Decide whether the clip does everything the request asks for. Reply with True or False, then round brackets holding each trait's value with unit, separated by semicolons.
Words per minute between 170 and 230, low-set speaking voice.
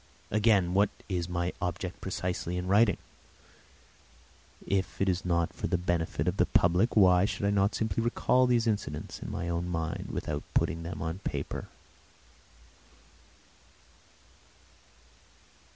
False (135 wpm; 90 Hz)